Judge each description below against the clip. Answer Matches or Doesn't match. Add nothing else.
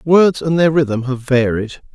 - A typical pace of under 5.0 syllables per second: Matches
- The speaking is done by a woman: Doesn't match